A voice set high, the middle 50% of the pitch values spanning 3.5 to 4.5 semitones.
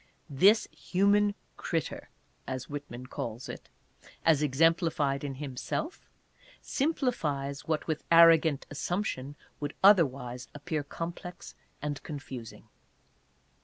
No: medium, 150 Hz; average, 3.9 semitones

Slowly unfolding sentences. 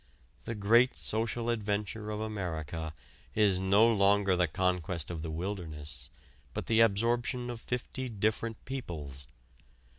Yes: slow, 125 wpm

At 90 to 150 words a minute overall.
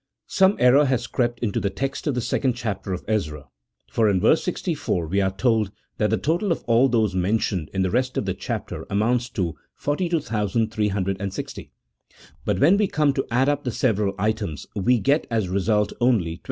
No: average, 190 wpm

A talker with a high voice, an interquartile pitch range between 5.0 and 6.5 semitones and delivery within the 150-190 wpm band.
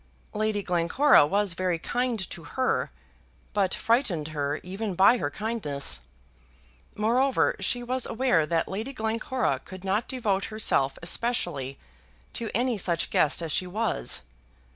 No: high, 205 Hz; wide, 5.5 semitones; slow, 135 wpm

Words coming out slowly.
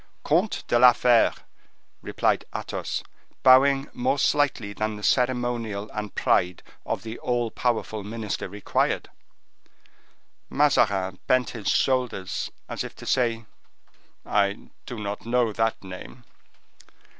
Yes: slow, 120 wpm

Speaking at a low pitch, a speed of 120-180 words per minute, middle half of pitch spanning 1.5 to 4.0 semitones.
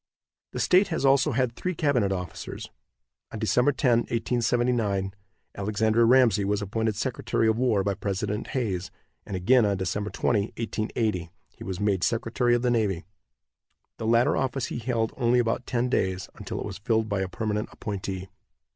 Yes: low, 110 Hz; average, 165 wpm; average, 3.5 semitones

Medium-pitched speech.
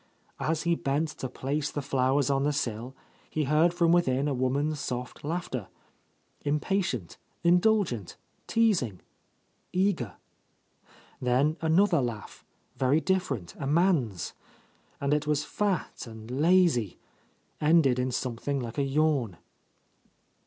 Yes: medium, 145 Hz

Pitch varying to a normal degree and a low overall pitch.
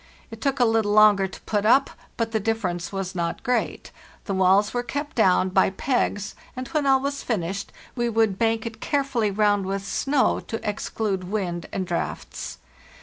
No: average, 3.9 semitones; high, 215 Hz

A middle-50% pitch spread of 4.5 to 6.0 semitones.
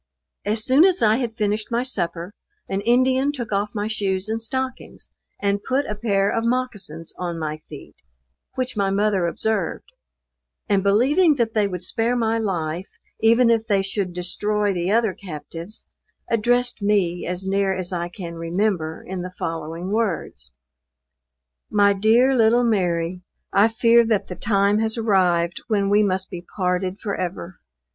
No: average, 3.9 semitones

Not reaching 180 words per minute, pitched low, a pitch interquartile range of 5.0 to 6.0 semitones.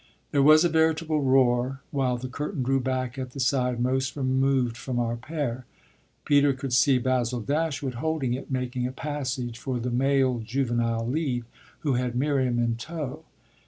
No: average, 165 wpm; low, 130 Hz; narrow, 2.4 semitones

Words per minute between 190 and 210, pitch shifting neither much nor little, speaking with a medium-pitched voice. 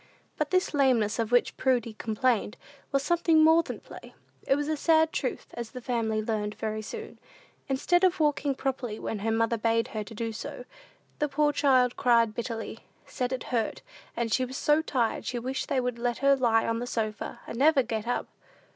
No: average, 200 wpm; average, 3.6 semitones; high, 245 Hz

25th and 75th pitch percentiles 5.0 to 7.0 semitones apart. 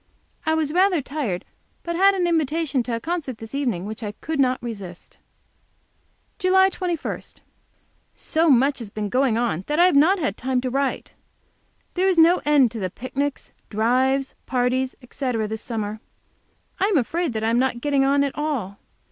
Yes: wide, 5.6 semitones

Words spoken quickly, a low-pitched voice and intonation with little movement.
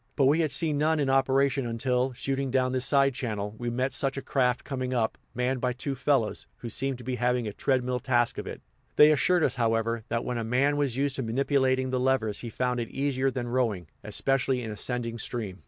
Yes: fast, 220 wpm; low, 130 Hz; narrow, 2.2 semitones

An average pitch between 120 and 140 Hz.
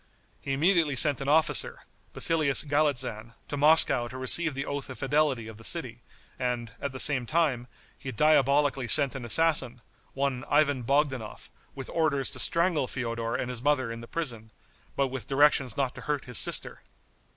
Yes: low, 135 Hz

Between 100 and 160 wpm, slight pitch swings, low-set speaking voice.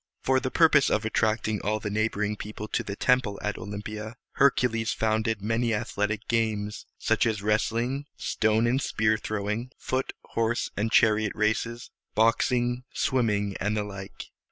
Yes: average, 155 wpm; narrow, 2.0 semitones; low, 110 Hz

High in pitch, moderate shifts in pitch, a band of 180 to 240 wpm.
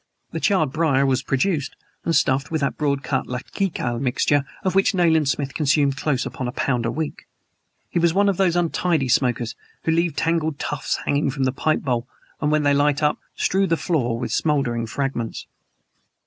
No: medium, 145 Hz; average, 3.8 semitones; average, 190 wpm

